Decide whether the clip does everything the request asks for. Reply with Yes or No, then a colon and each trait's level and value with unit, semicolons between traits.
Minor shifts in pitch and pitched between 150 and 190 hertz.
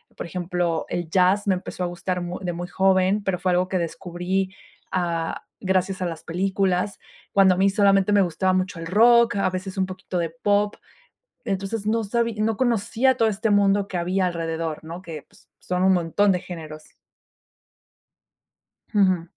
Yes: narrow, 2.2 semitones; medium, 185 Hz